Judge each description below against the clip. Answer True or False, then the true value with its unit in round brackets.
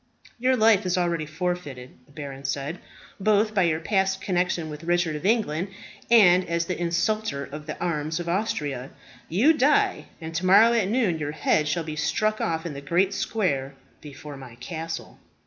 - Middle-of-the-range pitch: True (170 Hz)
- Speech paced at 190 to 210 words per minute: False (180 wpm)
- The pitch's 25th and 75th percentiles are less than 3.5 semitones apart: False (4.7 semitones)